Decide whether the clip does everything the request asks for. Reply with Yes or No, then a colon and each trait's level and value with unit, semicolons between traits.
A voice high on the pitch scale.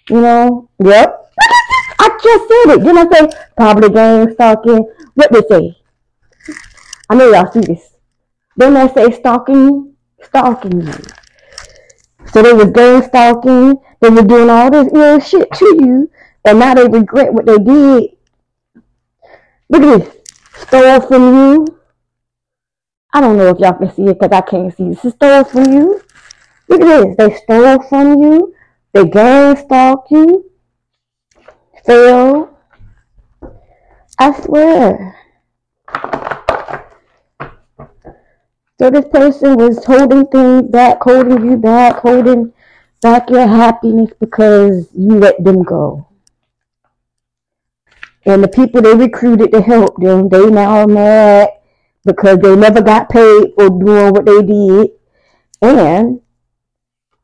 Yes: high, 240 Hz